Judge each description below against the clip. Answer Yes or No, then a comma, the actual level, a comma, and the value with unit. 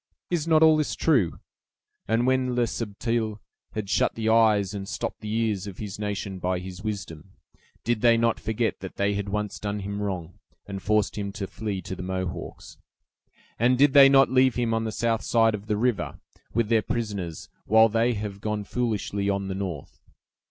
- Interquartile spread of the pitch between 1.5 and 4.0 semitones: Yes, average, 2.8 semitones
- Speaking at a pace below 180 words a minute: No, average, 195 wpm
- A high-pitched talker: No, low, 105 Hz